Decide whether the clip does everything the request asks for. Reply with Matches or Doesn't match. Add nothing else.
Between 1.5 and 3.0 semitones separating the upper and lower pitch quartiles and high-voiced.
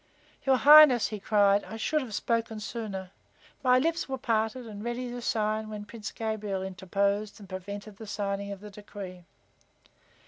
Matches